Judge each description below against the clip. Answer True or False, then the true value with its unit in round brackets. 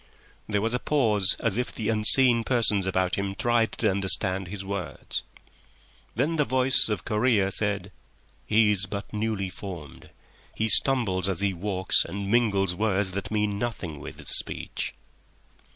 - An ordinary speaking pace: True (155 wpm)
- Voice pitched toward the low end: True (105 Hz)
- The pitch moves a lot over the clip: False (2.9 semitones)